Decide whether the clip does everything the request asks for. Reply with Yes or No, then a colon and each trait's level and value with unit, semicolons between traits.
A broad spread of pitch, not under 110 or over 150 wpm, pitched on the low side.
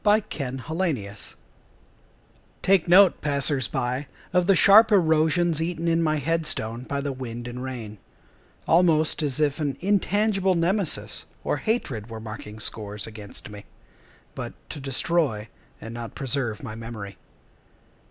No: wide, 6.9 semitones; average, 140 wpm; medium, 145 Hz